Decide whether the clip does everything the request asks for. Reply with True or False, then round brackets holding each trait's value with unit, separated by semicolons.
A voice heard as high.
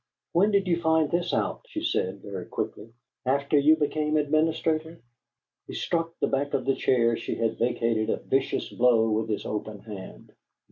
False (140 Hz)